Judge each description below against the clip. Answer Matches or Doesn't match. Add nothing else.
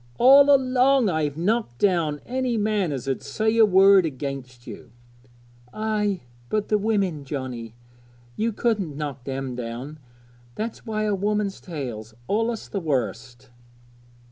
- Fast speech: Doesn't match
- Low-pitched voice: Doesn't match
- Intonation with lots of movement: Matches